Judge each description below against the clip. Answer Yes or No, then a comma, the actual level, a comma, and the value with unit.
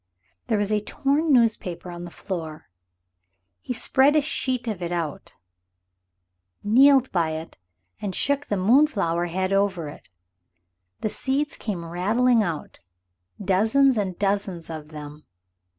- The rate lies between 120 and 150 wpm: Yes, slow, 135 wpm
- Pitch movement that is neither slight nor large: No, wide, 6.5 semitones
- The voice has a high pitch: Yes, high, 200 Hz